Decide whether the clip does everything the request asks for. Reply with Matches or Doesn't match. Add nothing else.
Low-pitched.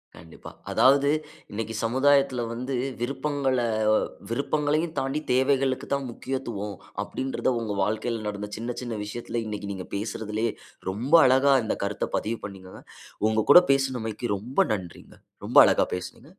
Matches